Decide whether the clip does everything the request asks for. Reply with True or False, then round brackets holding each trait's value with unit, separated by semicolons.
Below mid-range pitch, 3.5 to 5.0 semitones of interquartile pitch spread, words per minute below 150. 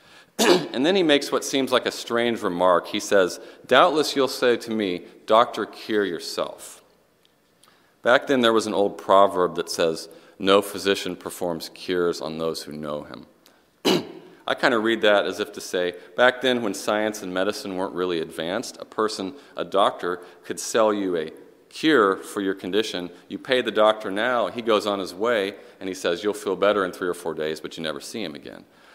False (100 Hz; 4.4 semitones; 195 wpm)